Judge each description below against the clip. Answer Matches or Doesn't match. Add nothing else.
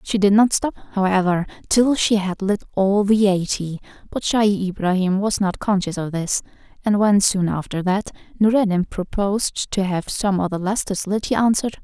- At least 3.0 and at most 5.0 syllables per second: Matches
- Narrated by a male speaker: Doesn't match